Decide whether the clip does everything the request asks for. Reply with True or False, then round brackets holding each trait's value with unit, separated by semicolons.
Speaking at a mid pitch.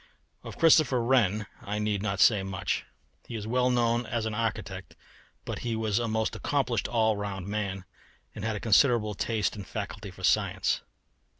False (110 Hz)